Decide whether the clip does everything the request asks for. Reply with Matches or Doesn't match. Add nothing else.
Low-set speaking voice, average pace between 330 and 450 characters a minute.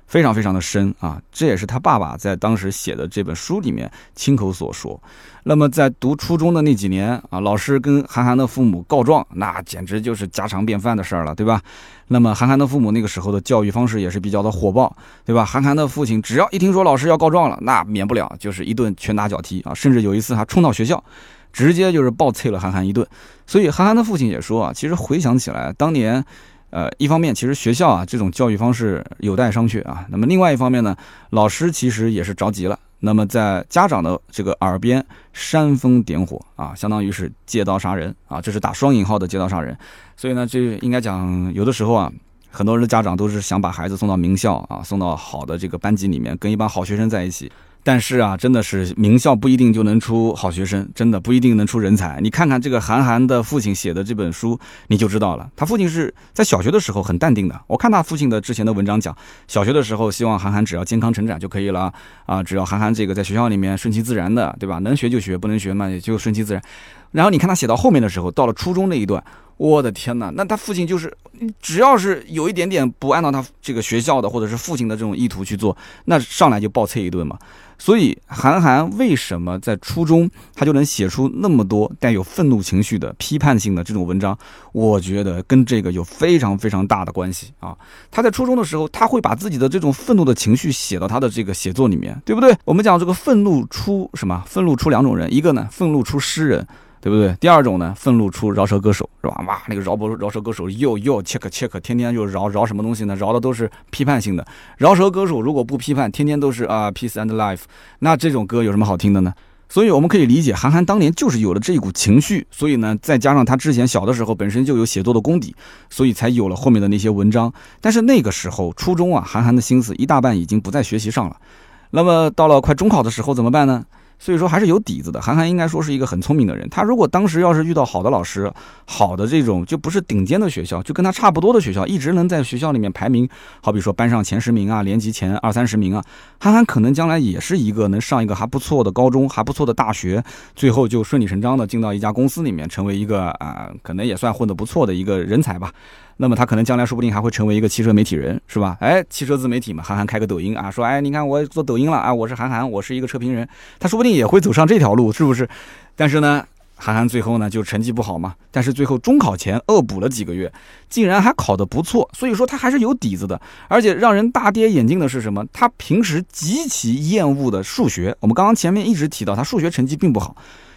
Matches